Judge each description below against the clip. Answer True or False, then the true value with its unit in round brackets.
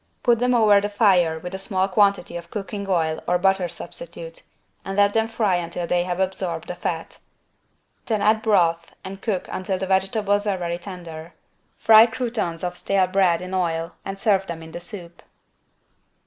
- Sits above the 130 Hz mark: True (190 Hz)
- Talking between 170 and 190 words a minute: True (180 wpm)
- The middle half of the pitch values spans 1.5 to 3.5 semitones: True (2.9 semitones)